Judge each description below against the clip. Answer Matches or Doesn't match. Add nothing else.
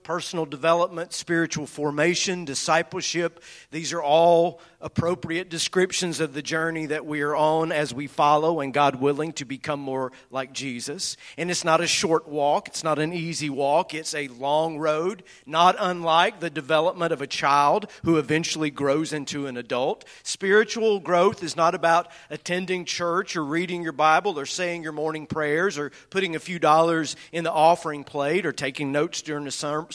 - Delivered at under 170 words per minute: Doesn't match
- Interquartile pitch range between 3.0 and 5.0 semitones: Doesn't match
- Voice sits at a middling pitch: Matches